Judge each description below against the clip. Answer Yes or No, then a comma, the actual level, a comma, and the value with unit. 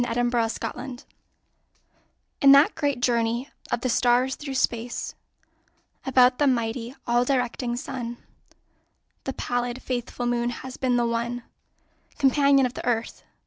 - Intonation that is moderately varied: No, narrow, 1.7 semitones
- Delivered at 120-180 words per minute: Yes, slow, 135 wpm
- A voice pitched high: Yes, high, 245 Hz